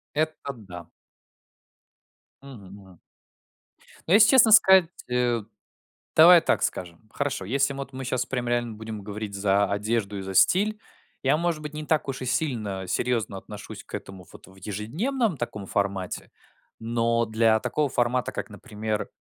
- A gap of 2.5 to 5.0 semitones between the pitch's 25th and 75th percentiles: No, wide, 5.6 semitones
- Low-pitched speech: Yes, low, 115 Hz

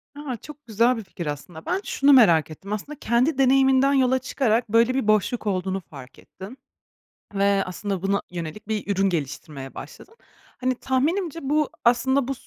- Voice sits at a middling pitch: No, high, 230 Hz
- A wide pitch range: Yes, wide, 5.7 semitones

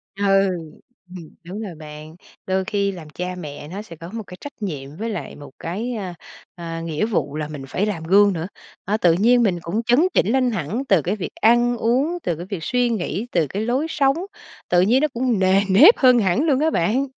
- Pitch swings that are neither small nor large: No, wide, 6.0 semitones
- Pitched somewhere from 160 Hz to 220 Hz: Yes, high, 195 Hz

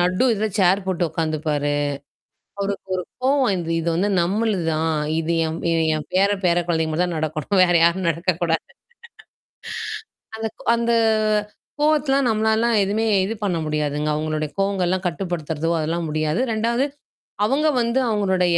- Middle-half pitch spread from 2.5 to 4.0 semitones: No, average, 4.7 semitones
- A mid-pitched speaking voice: Yes, medium, 180 Hz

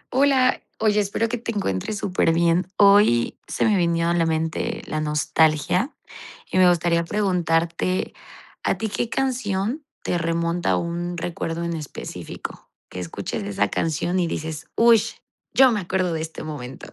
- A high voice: No, medium, 175 Hz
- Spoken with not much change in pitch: No, average, 4.1 semitones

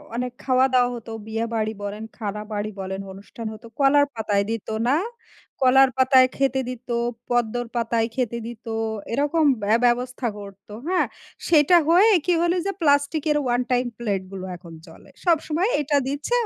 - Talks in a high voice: Yes, high, 245 Hz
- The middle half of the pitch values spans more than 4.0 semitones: Yes, average, 4.5 semitones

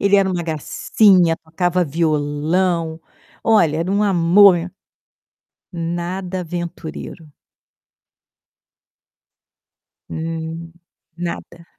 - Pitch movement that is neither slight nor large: No, narrow, 2.1 semitones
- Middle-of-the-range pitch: Yes, medium, 170 Hz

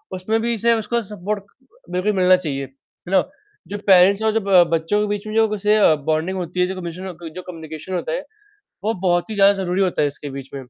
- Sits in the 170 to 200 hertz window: Yes, medium, 185 Hz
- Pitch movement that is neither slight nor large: Yes, average, 3.4 semitones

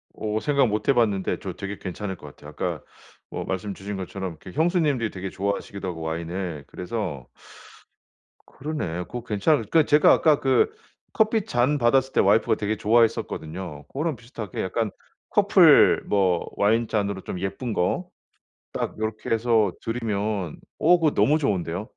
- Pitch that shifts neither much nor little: Yes, average, 4.7 semitones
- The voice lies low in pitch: Yes, low, 105 Hz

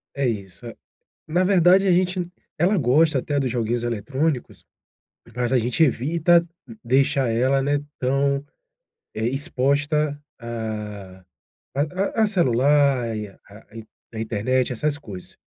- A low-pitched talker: Yes, low, 130 Hz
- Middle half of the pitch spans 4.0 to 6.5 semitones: Yes, average, 4.6 semitones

